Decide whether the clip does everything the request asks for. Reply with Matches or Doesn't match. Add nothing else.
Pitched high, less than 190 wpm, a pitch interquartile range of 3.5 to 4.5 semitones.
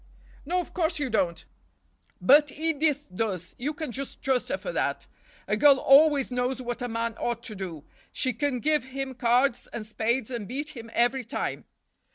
Matches